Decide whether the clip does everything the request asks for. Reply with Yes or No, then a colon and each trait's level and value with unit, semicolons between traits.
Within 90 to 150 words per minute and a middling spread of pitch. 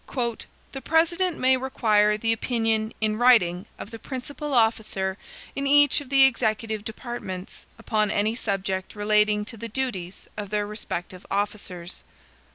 Yes: average, 140 wpm; average, 3.7 semitones